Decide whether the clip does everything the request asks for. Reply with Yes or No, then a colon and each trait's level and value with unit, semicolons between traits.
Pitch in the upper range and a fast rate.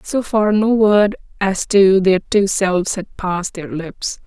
No: high, 195 Hz; average, 185 wpm